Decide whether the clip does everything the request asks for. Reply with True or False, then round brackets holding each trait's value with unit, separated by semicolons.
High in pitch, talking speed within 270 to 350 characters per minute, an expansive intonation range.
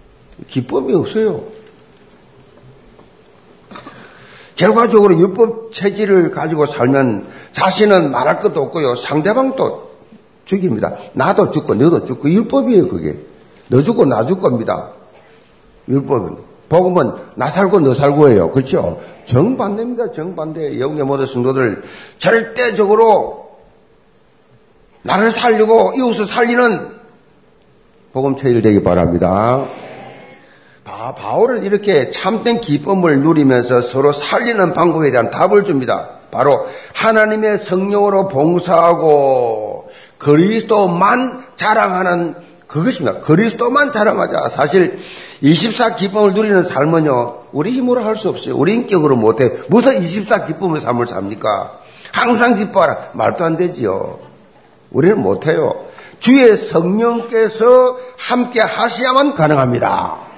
False (200 Hz; 260 characters per minute; 7.7 semitones)